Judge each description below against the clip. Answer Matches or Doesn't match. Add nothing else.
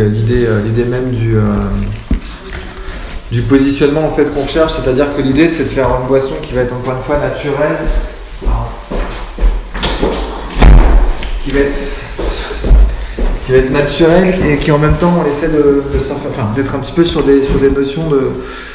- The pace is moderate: Matches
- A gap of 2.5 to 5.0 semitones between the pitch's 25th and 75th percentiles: Matches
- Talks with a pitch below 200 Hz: Matches